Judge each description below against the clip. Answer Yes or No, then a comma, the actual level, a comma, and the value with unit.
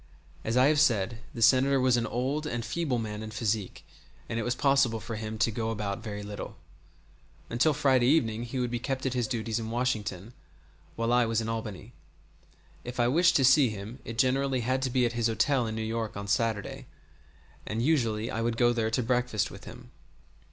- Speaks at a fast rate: Yes, fast, 210 wpm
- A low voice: Yes, low, 115 Hz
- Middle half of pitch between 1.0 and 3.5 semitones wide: Yes, narrow, 2.6 semitones